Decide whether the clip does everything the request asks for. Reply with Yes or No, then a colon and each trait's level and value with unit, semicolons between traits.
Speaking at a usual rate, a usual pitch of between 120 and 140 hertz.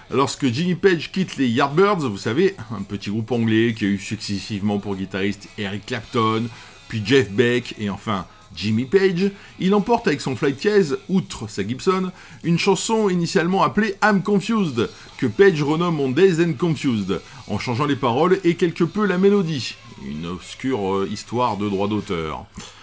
Yes: average, 170 wpm; low, 135 Hz